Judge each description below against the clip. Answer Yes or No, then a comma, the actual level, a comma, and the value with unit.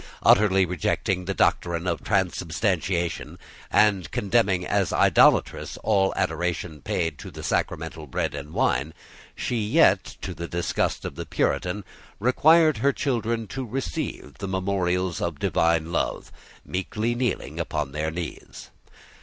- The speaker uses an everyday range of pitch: Yes, average, 4.1 semitones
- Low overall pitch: Yes, very low, 90 Hz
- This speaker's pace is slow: Yes, slow, 130 wpm